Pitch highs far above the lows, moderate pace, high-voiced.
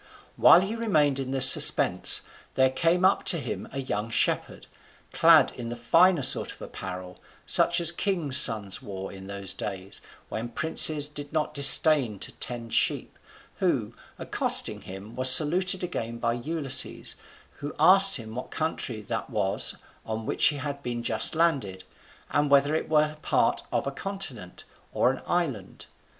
No: wide, 6.0 semitones; average, 160 wpm; low, 135 Hz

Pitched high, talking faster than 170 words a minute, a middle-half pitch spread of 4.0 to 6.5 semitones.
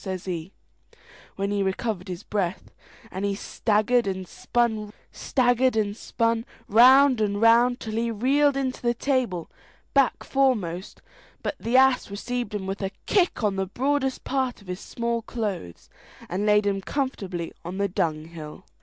No: high, 210 Hz; average, 145 wpm; average, 4.6 semitones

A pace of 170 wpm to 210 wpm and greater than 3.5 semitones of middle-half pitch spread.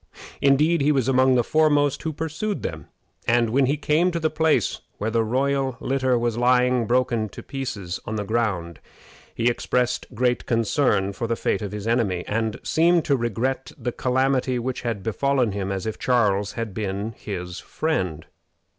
Yes: average, 175 wpm; average, 4.0 semitones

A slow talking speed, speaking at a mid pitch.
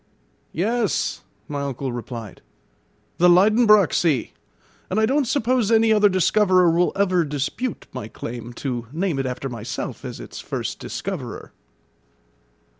Yes: slow, 130 wpm; medium, 180 Hz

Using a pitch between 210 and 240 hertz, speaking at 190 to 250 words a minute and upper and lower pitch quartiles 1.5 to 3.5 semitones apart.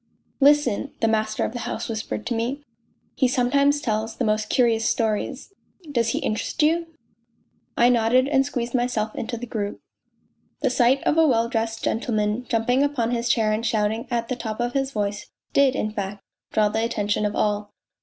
Yes: high, 230 Hz; average, 195 wpm; average, 2.9 semitones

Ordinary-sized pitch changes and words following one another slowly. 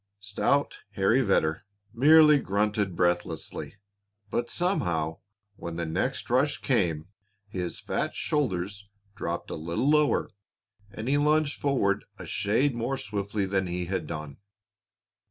No: wide, 7.6 semitones; slow, 125 wpm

